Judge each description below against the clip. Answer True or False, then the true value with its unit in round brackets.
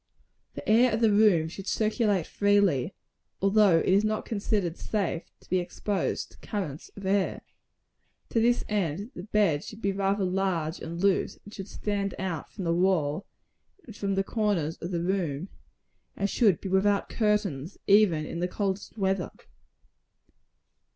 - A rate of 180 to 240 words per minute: False (160 wpm)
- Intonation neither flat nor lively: True (3.0 semitones)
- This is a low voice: False (195 Hz)